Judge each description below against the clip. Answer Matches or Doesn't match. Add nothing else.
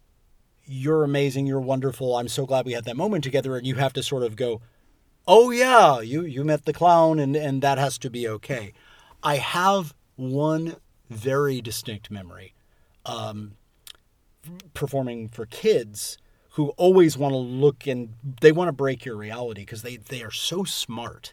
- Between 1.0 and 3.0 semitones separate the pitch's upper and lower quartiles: Doesn't match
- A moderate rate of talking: Matches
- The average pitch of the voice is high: Doesn't match